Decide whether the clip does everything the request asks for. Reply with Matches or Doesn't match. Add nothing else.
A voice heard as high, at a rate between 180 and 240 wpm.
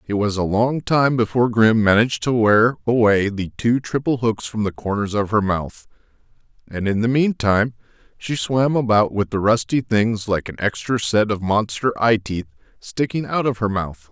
Doesn't match